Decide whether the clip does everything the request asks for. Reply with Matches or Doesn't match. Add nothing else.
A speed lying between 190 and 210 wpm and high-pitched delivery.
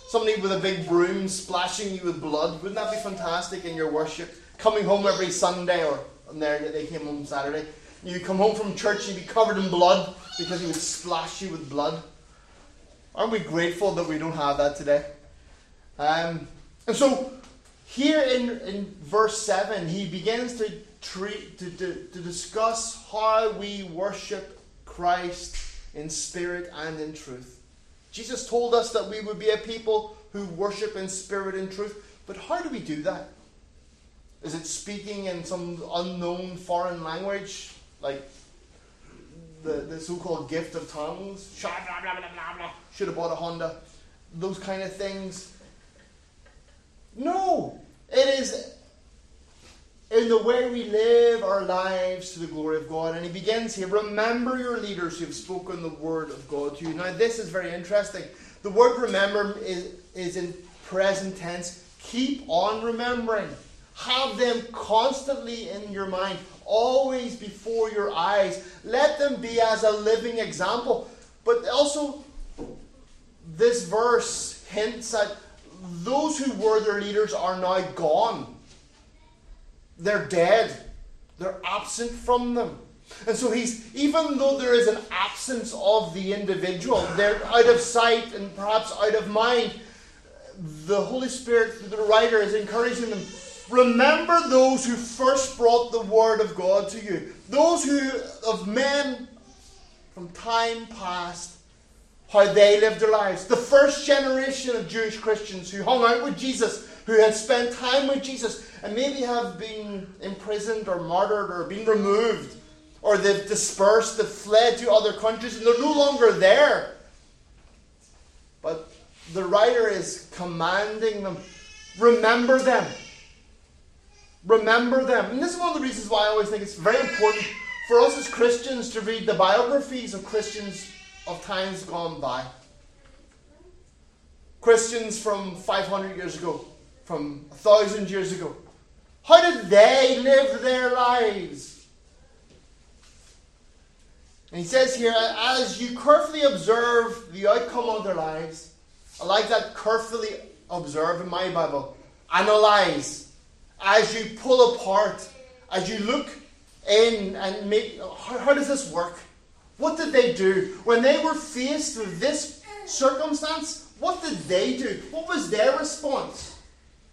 Doesn't match